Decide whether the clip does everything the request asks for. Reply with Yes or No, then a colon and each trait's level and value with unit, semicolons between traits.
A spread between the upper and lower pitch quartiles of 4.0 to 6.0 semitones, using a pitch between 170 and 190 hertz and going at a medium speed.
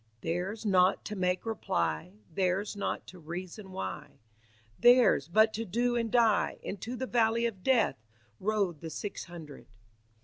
No: average, 4.4 semitones; high, 200 Hz; average, 145 wpm